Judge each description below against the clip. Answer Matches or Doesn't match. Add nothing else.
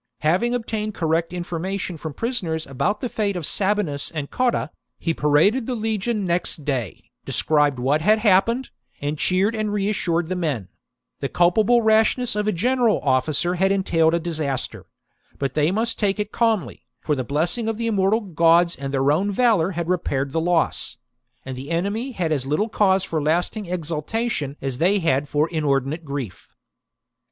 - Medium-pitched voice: Matches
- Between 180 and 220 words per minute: Doesn't match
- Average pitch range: Doesn't match